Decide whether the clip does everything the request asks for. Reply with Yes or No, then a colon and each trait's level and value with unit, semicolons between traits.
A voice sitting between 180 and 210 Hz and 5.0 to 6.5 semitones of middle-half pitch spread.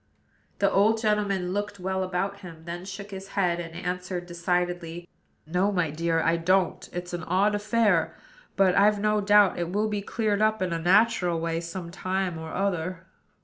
No: medium, 185 Hz; average, 2.7 semitones